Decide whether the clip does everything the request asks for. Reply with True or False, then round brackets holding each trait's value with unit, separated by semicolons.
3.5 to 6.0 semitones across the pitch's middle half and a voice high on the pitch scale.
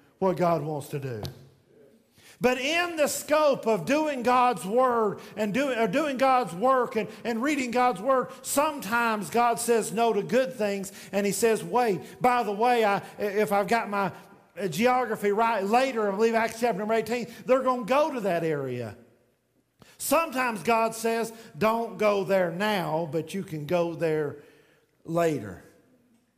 True (4.4 semitones; 225 Hz)